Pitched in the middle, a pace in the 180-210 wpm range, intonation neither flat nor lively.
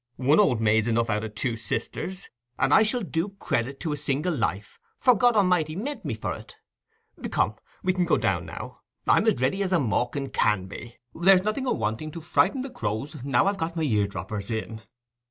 No: medium, 145 Hz; average, 200 wpm; wide, 8.8 semitones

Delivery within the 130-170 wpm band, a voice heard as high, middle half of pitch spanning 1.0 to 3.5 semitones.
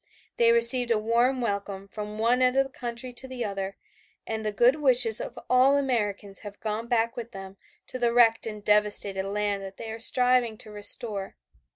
No: average, 195 wpm; high, 225 Hz; average, 2.9 semitones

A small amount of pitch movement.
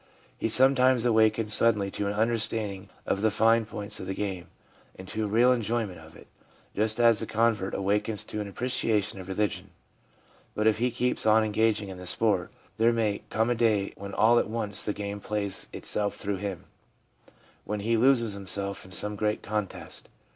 Yes: narrow, 2.2 semitones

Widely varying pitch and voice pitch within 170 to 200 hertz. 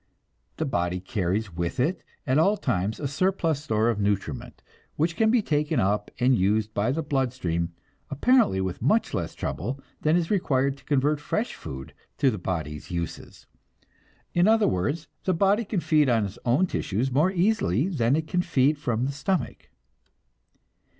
No: wide, 8.3 semitones; low, 130 Hz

